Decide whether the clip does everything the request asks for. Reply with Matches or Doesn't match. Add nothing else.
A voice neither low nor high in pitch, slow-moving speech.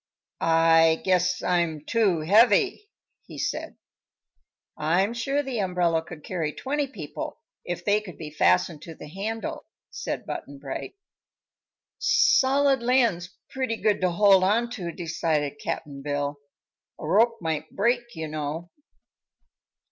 Matches